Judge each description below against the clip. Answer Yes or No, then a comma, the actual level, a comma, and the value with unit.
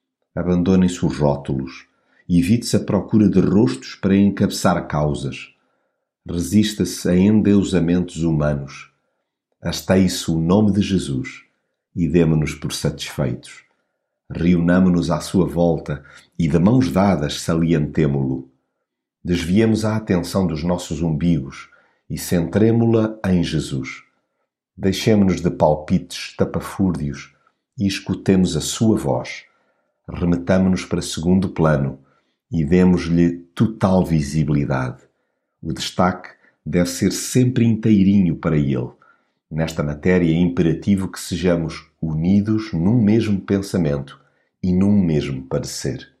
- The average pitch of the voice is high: No, very low, 90 Hz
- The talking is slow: Yes, slow, 110 wpm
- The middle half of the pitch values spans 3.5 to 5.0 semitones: Yes, average, 3.8 semitones